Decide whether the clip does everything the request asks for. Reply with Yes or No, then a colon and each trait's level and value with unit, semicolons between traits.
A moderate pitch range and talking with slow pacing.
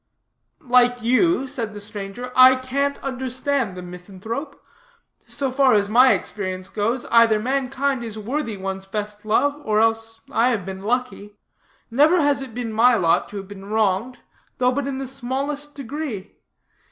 No: average, 4.3 semitones; average, 160 wpm